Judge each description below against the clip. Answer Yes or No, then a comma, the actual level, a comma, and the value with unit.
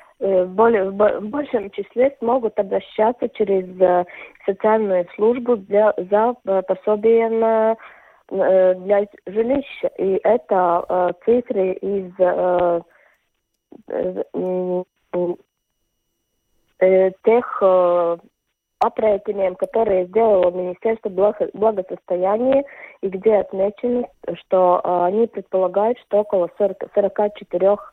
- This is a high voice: Yes, high, 205 Hz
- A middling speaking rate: No, slow, 85 wpm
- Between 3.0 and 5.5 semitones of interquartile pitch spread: Yes, average, 3.3 semitones